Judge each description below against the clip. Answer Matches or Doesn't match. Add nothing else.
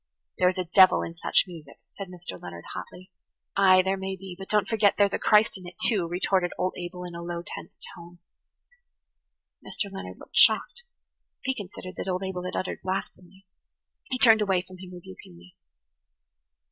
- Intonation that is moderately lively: Doesn't match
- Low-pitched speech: Doesn't match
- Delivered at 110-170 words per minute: Doesn't match